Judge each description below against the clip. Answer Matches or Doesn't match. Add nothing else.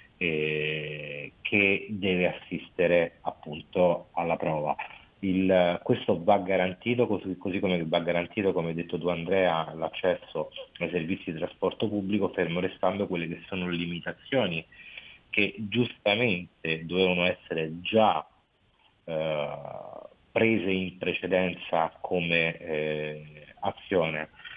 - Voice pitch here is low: Matches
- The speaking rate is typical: Doesn't match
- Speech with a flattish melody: Doesn't match